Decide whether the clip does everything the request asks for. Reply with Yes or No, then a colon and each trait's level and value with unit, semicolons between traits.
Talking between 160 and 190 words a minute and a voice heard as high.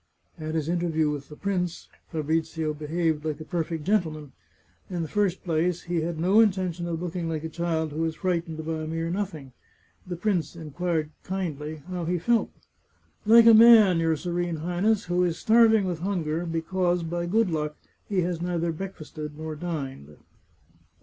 No: average, 175 wpm; medium, 170 Hz